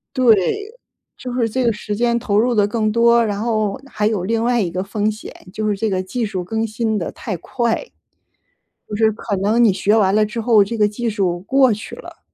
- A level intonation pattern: Yes, narrow, 2.3 semitones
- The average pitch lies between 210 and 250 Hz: Yes, high, 215 Hz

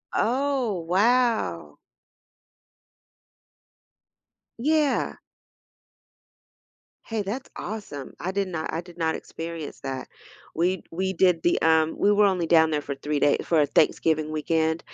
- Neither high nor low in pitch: Yes, medium, 170 Hz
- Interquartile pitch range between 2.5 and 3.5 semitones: No, average, 4.6 semitones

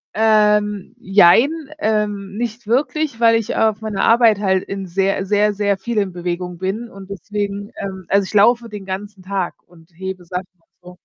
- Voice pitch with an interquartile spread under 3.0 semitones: Yes, narrow, 2.4 semitones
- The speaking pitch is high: Yes, high, 200 Hz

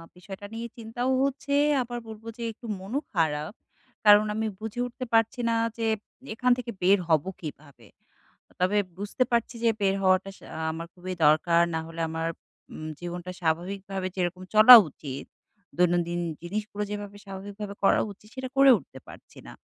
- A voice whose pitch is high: Yes, high, 195 Hz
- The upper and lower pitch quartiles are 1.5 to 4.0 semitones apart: No, average, 4.6 semitones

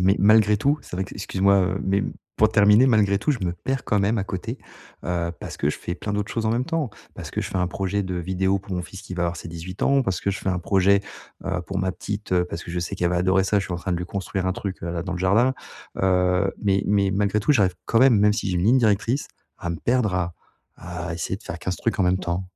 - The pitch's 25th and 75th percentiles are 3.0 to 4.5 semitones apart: No, narrow, 2.5 semitones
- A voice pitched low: Yes, very low, 95 Hz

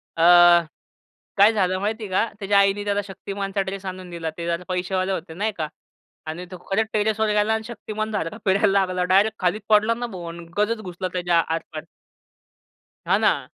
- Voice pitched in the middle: No, high, 195 Hz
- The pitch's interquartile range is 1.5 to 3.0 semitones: Yes, average, 2.7 semitones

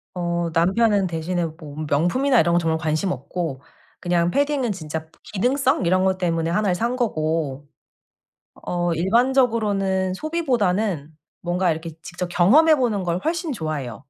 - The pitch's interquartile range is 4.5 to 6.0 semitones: Yes, wide, 5.4 semitones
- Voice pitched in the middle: Yes, medium, 180 Hz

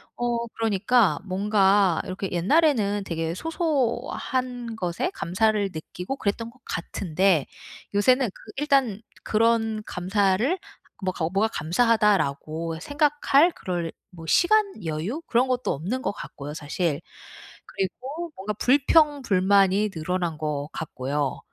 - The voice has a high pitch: Yes, high, 205 Hz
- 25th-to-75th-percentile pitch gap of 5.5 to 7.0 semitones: Yes, wide, 6.3 semitones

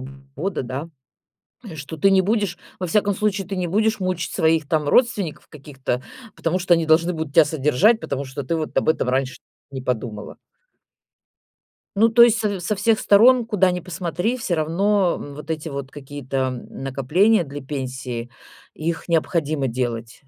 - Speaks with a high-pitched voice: No, medium, 160 Hz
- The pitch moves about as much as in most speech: No, wide, 6.0 semitones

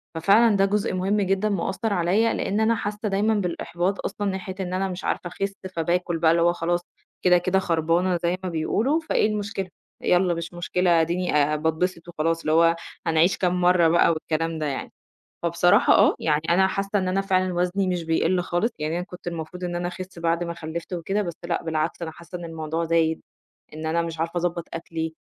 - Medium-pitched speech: Yes, medium, 175 Hz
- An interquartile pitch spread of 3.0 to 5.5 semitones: No, narrow, 2.4 semitones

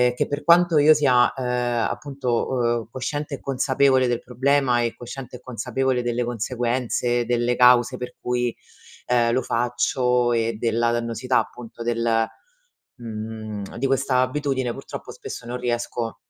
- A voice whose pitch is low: Yes, low, 125 Hz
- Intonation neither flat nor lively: No, narrow, 1.8 semitones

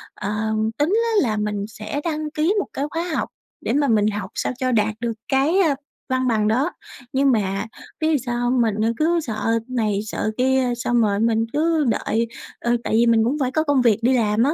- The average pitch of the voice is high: Yes, high, 240 Hz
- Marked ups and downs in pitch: No, average, 4.6 semitones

